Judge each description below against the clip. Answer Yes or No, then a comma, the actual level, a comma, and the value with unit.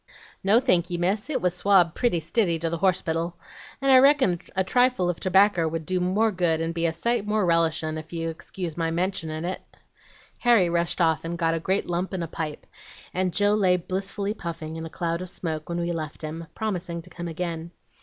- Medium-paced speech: No, fast, 210 wpm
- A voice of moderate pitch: Yes, medium, 175 Hz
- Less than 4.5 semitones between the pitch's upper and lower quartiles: Yes, narrow, 2.5 semitones